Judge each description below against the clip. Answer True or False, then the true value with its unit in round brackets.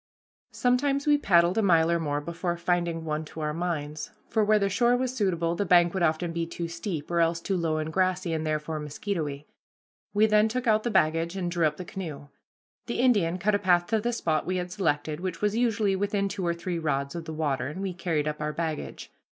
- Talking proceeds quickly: True (230 wpm)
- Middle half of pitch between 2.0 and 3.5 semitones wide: False (4.0 semitones)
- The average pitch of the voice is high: False (175 Hz)